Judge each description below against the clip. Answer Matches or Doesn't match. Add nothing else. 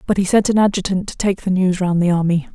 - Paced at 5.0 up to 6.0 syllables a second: Doesn't match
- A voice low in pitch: Doesn't match